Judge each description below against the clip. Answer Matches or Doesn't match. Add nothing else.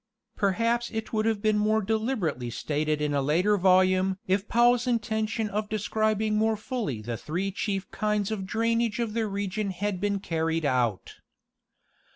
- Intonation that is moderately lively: Matches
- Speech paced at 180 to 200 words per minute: Doesn't match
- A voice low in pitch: Doesn't match